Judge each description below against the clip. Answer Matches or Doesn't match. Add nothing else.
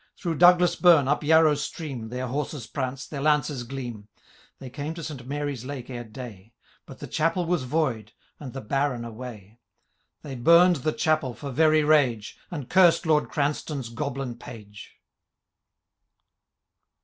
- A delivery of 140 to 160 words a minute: Matches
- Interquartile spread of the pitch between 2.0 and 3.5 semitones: Doesn't match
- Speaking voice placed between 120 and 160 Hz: Matches